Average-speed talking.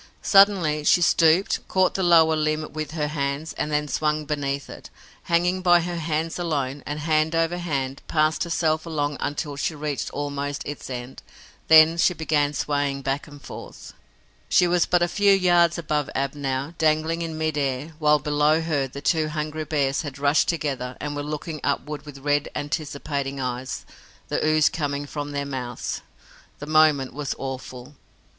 Yes: average, 170 wpm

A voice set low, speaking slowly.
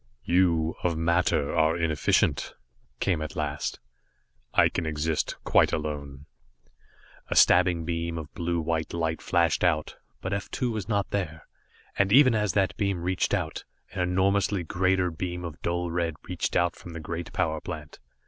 No: very low, 85 Hz; average, 160 wpm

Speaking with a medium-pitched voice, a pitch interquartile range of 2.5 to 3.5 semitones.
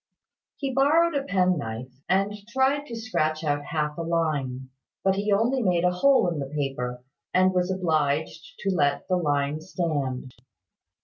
No: medium, 170 Hz; wide, 5.6 semitones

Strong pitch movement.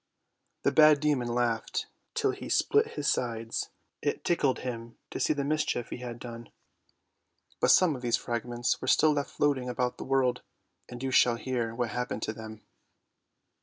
No: average, 3.4 semitones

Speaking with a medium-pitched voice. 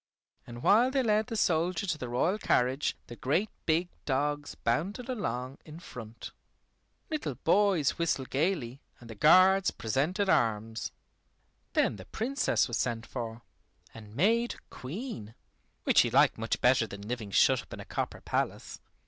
Yes: medium, 145 Hz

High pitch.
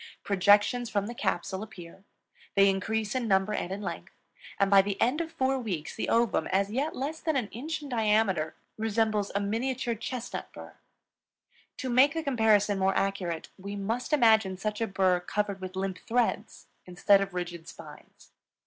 Yes: high, 210 Hz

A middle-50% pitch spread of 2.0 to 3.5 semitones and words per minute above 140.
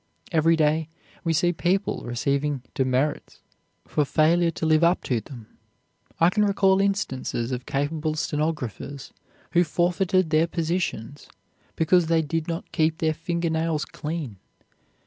No: average, 2.8 semitones; slow, 135 wpm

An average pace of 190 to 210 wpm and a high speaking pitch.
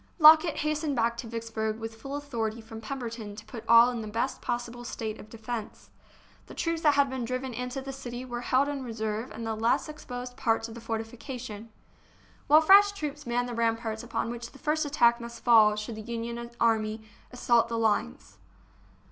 Yes: average, 195 wpm; high, 235 Hz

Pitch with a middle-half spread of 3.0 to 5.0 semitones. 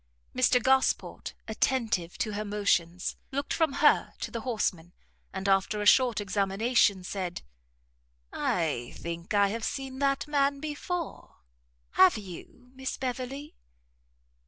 No: wide, 5.6 semitones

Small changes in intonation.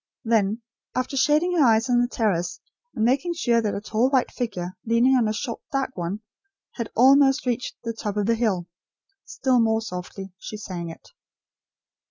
No: average, 3.7 semitones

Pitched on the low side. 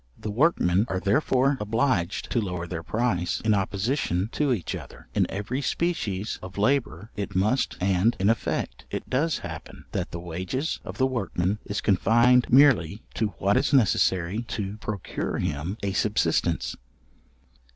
Yes: low, 105 Hz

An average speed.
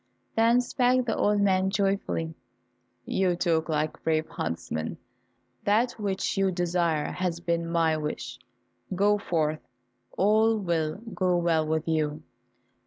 No: slow, 125 wpm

